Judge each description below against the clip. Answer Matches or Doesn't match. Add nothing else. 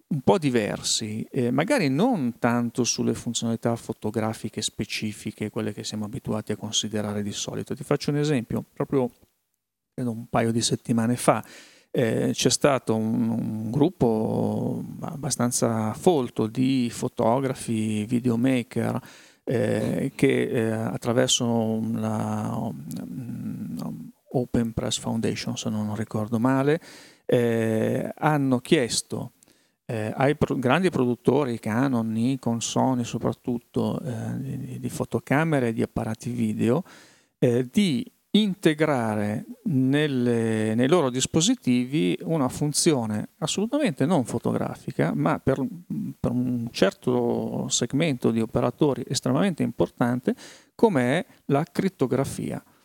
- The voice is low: Matches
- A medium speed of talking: Doesn't match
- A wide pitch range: Doesn't match